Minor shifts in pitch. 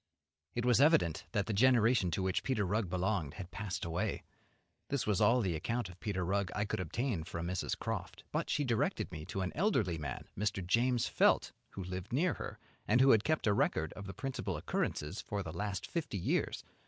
No: average, 4.8 semitones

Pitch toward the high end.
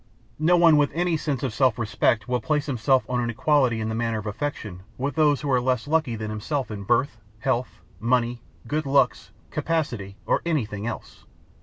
No: low, 125 Hz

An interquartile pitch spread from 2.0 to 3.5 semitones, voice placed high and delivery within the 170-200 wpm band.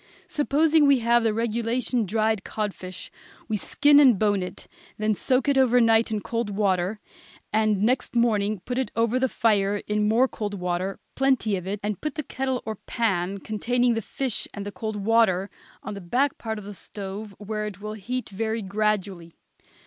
Yes: average, 3.1 semitones; high, 215 Hz; average, 185 wpm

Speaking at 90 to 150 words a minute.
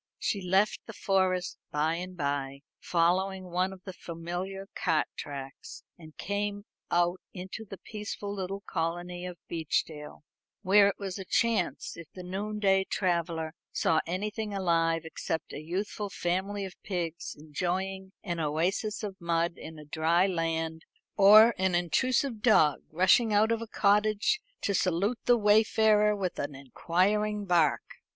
Yes: average, 145 wpm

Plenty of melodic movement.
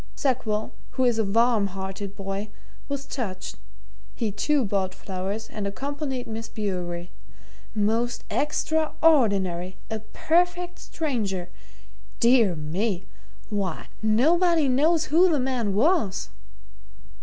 Yes: wide, 6.3 semitones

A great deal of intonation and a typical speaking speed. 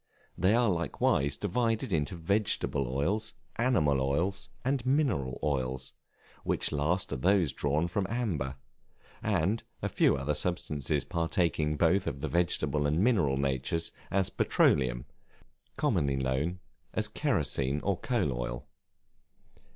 No: wide, 6.2 semitones; slow, 125 wpm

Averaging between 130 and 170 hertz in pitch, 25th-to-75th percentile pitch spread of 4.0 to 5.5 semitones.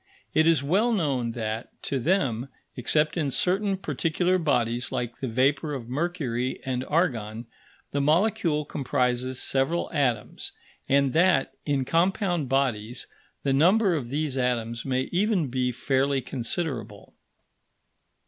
Yes: low, 135 Hz; average, 4.9 semitones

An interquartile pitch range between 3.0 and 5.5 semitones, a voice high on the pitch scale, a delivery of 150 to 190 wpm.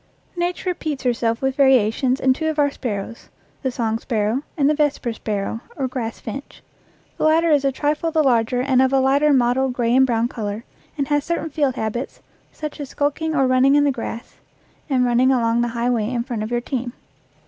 No: average, 3.3 semitones; very high, 260 Hz; fast, 205 wpm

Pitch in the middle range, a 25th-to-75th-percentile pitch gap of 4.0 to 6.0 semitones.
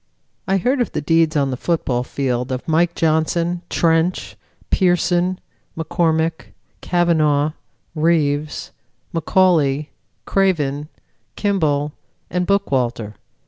No: medium, 160 Hz; average, 3.4 semitones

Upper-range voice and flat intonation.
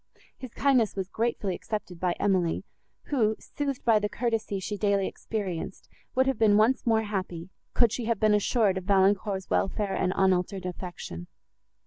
No: high, 205 Hz; average, 3.1 semitones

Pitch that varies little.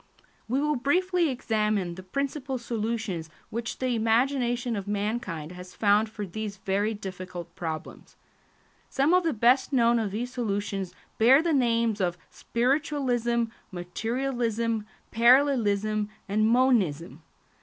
No: average, 4.0 semitones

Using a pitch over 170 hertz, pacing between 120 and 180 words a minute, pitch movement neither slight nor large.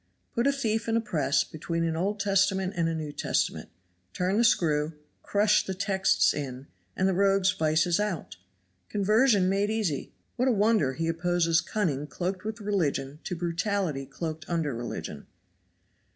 Yes: medium, 185 Hz; average, 160 wpm; average, 4.5 semitones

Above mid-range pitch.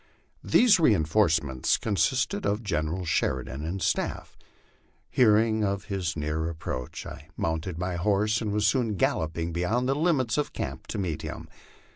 No: very low, 95 Hz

